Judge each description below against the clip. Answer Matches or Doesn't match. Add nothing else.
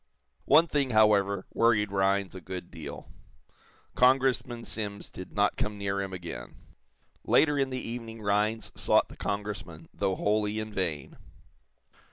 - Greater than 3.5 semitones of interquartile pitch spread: Doesn't match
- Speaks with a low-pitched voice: Matches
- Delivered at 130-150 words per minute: Matches